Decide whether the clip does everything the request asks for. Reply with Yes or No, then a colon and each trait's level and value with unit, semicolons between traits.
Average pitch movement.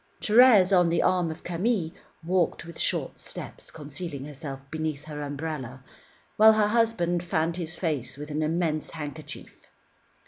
Yes: average, 3.4 semitones